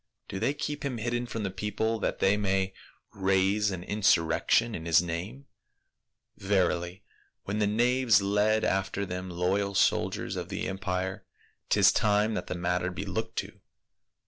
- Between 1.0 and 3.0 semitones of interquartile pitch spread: Yes, narrow, 2.6 semitones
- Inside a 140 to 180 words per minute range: Yes, average, 165 wpm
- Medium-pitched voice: No, low, 100 Hz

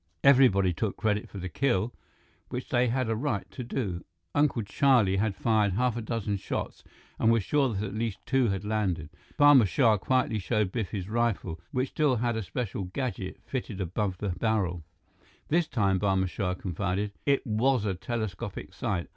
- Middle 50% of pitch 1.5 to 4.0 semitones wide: No, average, 4.4 semitones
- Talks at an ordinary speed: Yes, average, 180 wpm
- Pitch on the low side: Yes, low, 110 Hz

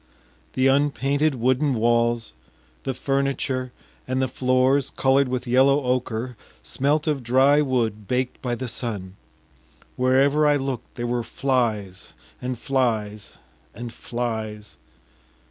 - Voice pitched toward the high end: No, low, 130 Hz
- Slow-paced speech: Yes, slow, 120 wpm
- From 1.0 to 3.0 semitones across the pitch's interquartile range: Yes, narrow, 2.5 semitones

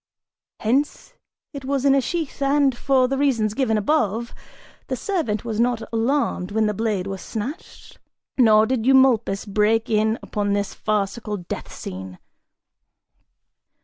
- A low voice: No, high, 225 Hz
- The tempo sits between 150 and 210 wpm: No, average, 140 wpm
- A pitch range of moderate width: Yes, average, 4.2 semitones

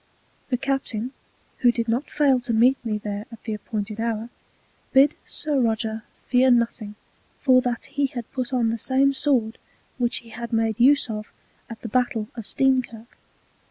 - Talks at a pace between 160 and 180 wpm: Yes, average, 170 wpm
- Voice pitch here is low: No, high, 240 Hz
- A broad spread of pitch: No, average, 2.8 semitones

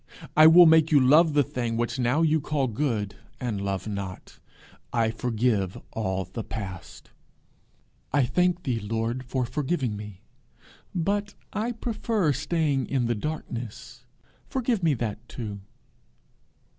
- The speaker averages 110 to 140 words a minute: Yes, slow, 135 wpm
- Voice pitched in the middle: No, low, 125 Hz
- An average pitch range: No, wide, 6.1 semitones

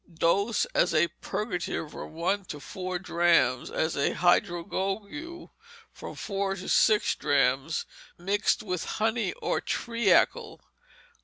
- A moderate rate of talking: No, slow, 120 wpm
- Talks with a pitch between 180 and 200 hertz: Yes, medium, 185 Hz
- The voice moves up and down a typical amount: Yes, average, 3.7 semitones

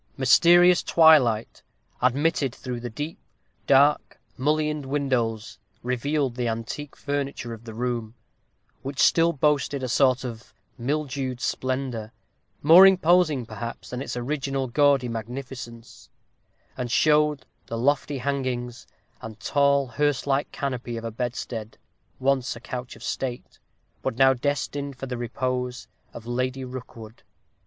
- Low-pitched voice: Yes, low, 130 Hz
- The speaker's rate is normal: No, slow, 130 wpm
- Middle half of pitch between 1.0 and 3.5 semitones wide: Yes, average, 2.9 semitones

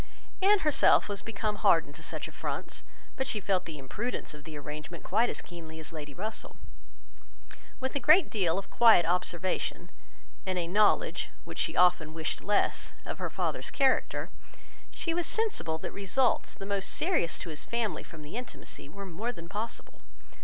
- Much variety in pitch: Yes, wide, 6.1 semitones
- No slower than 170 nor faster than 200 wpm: Yes, average, 175 wpm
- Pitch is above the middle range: Yes, high, 195 Hz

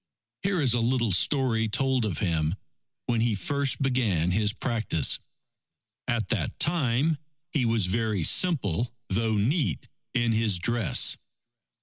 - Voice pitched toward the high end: No, low, 115 Hz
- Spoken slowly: Yes, slow, 130 wpm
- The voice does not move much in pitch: No, average, 4.2 semitones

